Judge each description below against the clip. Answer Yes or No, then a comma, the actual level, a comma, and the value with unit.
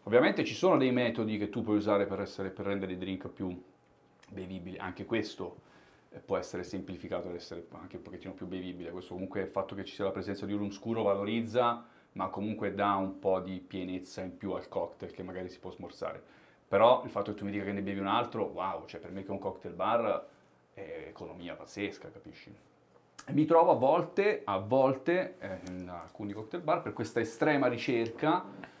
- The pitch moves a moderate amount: No, narrow, 2.2 semitones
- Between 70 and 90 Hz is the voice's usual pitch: No, low, 100 Hz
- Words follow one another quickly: Yes, fast, 205 wpm